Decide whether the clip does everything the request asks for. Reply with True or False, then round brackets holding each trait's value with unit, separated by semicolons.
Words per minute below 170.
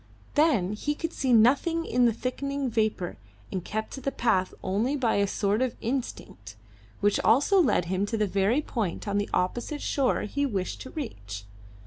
False (180 wpm)